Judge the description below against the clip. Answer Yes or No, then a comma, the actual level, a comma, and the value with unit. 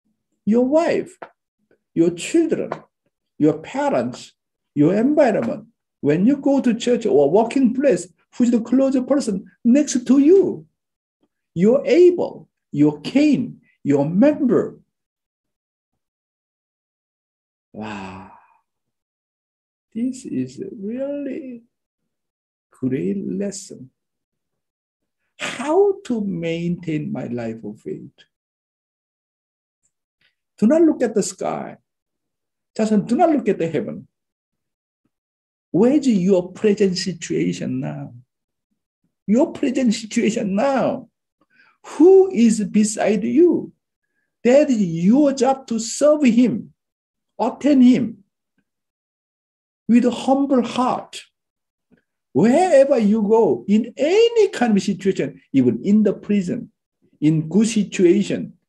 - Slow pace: Yes, slow, 100 wpm